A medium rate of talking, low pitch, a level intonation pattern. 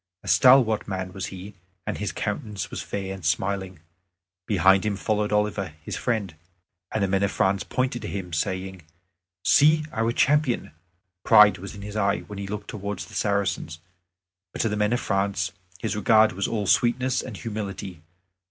Yes: average, 175 wpm; low, 100 Hz; narrow, 2.3 semitones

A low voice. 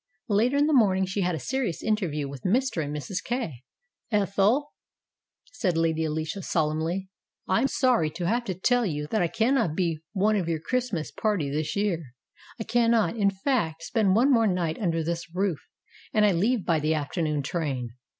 No: medium, 185 Hz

